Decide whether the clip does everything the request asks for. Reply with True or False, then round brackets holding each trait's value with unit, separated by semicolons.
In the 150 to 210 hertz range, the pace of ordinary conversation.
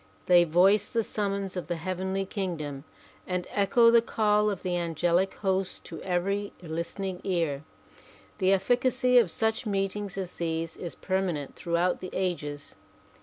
True (185 Hz; 150 wpm)